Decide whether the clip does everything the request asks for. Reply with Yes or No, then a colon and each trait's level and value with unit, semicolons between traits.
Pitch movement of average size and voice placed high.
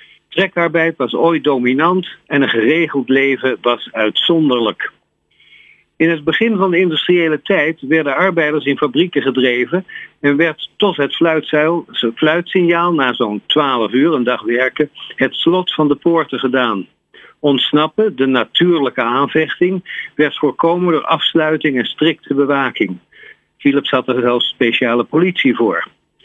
No: average, 4.3 semitones; medium, 150 Hz